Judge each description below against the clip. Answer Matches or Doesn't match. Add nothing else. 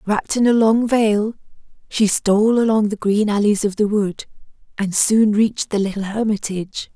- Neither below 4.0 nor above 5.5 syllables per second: Matches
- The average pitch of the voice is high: Matches